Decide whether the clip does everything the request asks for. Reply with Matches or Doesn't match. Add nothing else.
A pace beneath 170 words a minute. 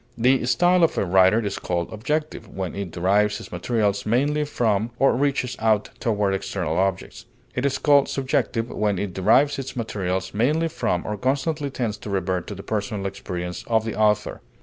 Doesn't match